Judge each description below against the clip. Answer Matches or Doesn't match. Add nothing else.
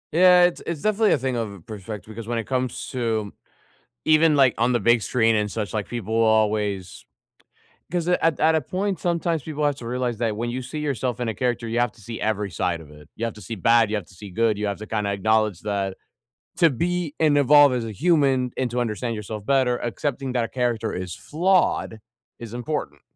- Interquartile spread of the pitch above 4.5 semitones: Matches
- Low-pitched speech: Matches